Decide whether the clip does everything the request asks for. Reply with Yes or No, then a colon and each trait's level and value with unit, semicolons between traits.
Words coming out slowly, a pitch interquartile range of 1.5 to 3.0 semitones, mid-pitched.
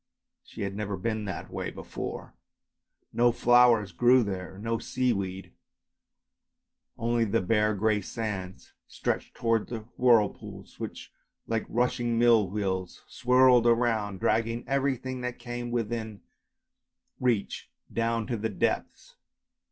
No: slow, 120 wpm; average, 2.7 semitones; low, 115 Hz